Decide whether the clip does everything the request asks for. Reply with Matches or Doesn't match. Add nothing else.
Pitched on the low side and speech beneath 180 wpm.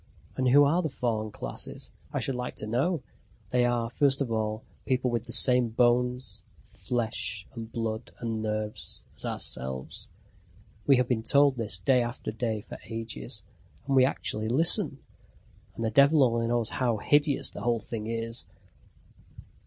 Matches